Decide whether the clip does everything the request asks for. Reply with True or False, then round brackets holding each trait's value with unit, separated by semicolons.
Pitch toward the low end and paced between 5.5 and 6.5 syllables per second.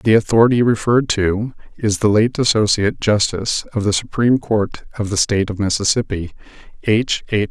True (110 Hz; 5.7 syllables/s)